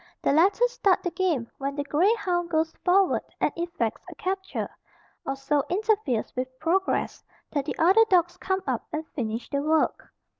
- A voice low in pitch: No, very high, 340 Hz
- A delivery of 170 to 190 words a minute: Yes, average, 175 wpm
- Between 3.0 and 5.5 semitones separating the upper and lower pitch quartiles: Yes, average, 5.1 semitones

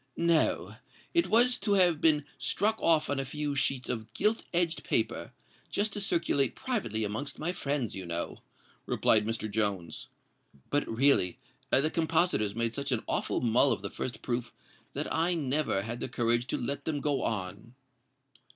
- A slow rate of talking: No, average, 160 wpm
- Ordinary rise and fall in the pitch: No, wide, 6.6 semitones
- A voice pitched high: No, medium, 140 Hz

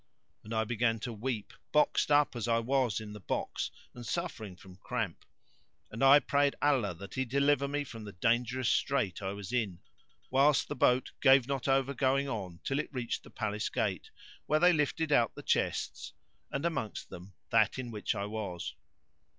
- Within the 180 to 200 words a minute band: Yes, average, 185 wpm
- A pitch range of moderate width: Yes, average, 4.6 semitones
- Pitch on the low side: Yes, low, 120 Hz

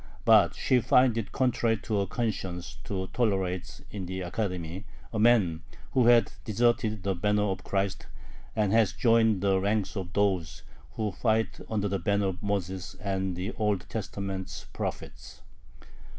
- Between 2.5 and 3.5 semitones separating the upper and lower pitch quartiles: Yes, average, 2.8 semitones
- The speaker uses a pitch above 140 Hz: No, low, 100 Hz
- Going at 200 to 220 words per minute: No, average, 150 wpm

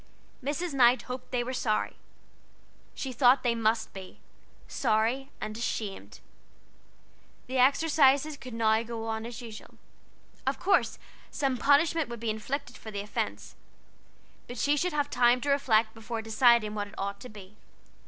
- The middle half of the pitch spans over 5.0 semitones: No, average, 3.7 semitones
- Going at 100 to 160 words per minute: Yes, average, 150 wpm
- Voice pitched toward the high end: Yes, high, 240 Hz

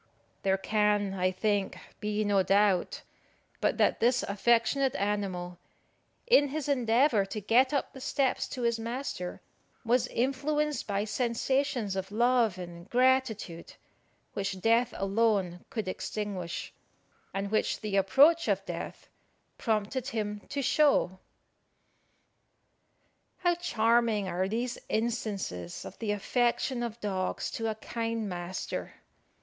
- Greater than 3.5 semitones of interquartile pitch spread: Yes, average, 4.1 semitones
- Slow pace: Yes, slow, 120 wpm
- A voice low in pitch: No, high, 220 Hz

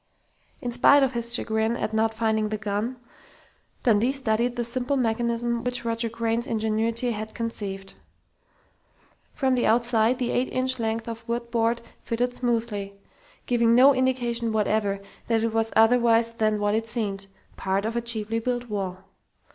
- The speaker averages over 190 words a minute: No, average, 155 wpm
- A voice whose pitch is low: No, high, 230 Hz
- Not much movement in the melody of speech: Yes, narrow, 1.7 semitones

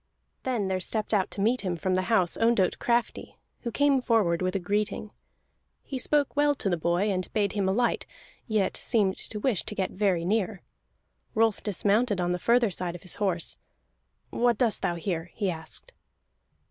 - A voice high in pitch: Yes, high, 205 Hz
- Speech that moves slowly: No, average, 185 wpm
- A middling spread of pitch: Yes, average, 3.9 semitones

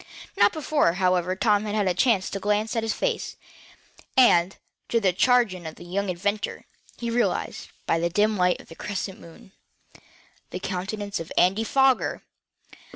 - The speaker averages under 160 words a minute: No, average, 165 wpm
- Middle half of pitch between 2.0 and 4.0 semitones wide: Yes, average, 3.5 semitones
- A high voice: Yes, high, 200 Hz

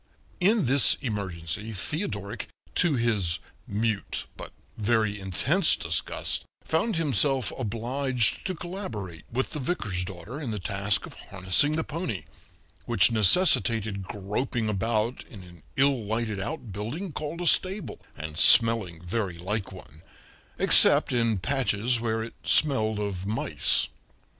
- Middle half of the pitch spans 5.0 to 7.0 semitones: Yes, wide, 5.5 semitones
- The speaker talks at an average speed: No, slow, 130 wpm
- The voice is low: Yes, low, 110 Hz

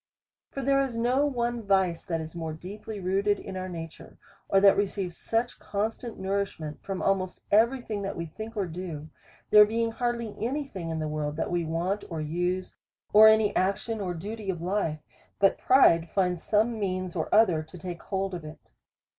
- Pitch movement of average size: Yes, average, 4.3 semitones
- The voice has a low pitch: No, high, 195 Hz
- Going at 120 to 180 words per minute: No, average, 195 wpm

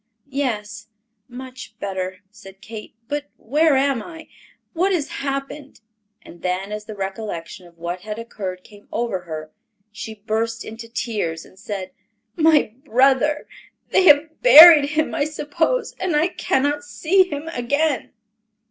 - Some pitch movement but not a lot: No, wide, 6.4 semitones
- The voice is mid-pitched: No, high, 240 Hz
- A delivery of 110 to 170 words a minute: Yes, average, 140 wpm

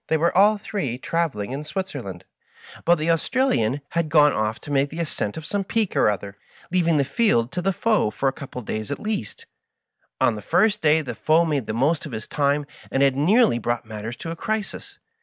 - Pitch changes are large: Yes, wide, 6.4 semitones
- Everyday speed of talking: No, fast, 220 wpm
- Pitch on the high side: No, medium, 150 Hz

